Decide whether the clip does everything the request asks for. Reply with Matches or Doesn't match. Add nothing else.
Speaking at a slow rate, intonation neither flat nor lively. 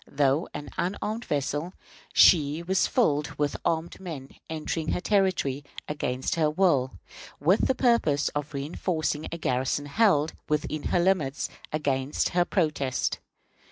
Matches